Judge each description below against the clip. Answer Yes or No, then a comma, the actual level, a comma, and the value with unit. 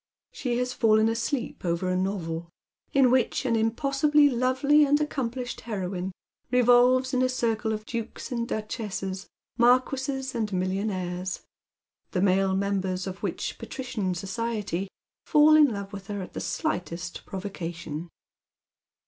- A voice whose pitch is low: No, high, 220 Hz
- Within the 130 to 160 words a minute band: Yes, slow, 135 wpm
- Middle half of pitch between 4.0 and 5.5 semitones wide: Yes, average, 5.2 semitones